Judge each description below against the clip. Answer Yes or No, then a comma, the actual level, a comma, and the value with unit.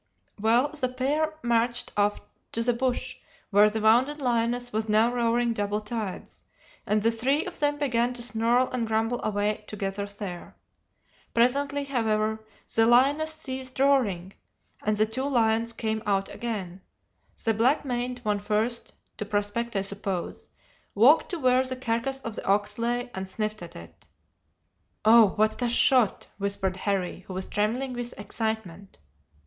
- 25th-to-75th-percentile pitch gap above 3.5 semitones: No, average, 3.2 semitones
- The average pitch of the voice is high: Yes, high, 230 Hz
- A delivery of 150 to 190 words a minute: Yes, average, 155 wpm